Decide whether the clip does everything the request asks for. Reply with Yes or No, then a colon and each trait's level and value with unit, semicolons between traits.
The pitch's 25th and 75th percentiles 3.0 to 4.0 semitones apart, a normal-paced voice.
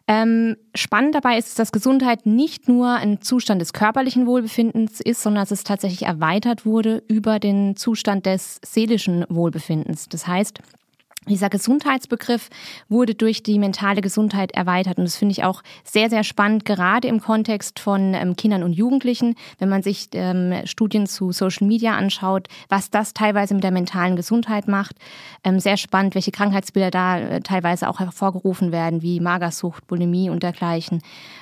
Yes: average, 3.3 semitones; average, 155 wpm